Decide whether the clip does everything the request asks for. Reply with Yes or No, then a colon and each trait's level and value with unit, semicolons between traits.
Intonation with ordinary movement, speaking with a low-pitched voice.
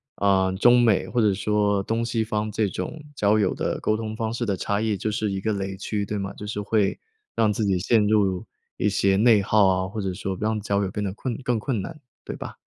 No: narrow, 2.0 semitones; low, 105 Hz